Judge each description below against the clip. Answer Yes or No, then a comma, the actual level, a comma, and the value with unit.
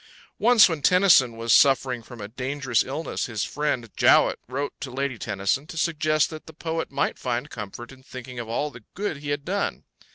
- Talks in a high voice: No, low, 135 Hz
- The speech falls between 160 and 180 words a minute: No, average, 195 wpm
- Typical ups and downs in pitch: Yes, average, 4.3 semitones